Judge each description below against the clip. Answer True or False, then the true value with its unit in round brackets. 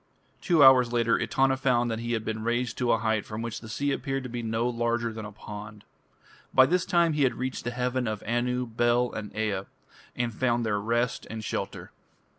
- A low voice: True (120 Hz)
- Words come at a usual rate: False (215 wpm)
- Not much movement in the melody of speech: True (2.2 semitones)